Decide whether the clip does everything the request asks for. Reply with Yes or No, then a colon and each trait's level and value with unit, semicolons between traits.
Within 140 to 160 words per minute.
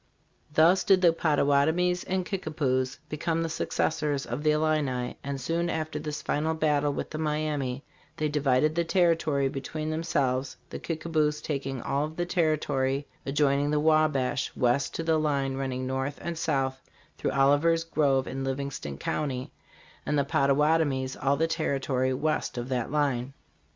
Yes: average, 155 wpm